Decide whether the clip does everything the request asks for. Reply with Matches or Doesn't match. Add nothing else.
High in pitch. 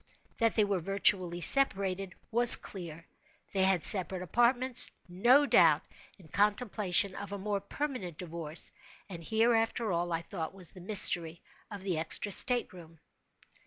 Matches